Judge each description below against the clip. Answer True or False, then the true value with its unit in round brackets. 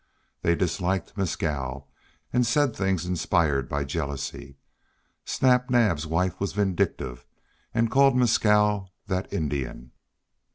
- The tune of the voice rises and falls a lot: True (6.6 semitones)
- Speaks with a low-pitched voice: True (90 Hz)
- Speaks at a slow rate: True (110 wpm)